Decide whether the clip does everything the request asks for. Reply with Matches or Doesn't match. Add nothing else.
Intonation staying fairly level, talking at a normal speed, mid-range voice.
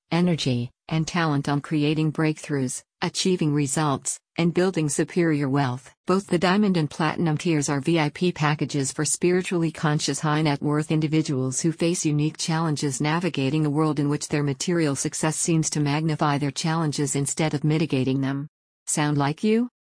Matches